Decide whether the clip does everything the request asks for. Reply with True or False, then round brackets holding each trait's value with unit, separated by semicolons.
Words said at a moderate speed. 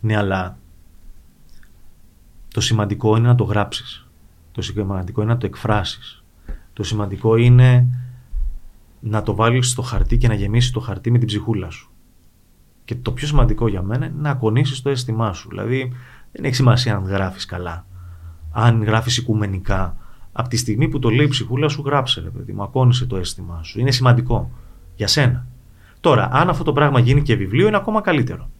False (180 wpm)